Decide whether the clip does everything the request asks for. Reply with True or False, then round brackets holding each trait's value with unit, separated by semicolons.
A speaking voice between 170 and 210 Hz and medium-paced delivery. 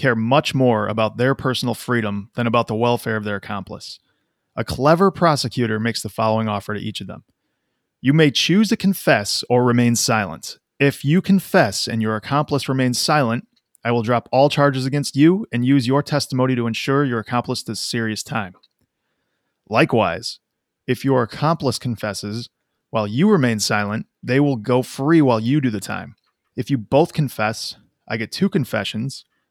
False (125 Hz; 175 wpm)